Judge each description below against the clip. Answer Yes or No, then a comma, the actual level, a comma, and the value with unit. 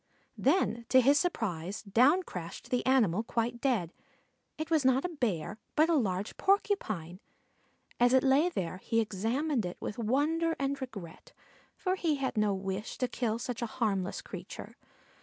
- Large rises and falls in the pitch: Yes, wide, 5.9 semitones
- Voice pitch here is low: No, high, 240 Hz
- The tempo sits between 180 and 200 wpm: No, average, 160 wpm